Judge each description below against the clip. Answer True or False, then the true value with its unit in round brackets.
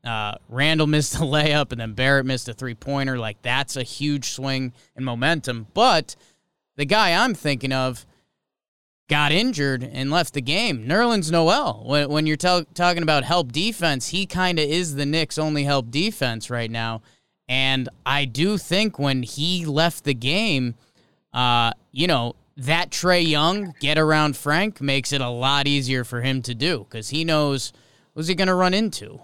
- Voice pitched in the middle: True (145 Hz)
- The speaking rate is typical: True (180 wpm)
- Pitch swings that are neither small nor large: True (4.2 semitones)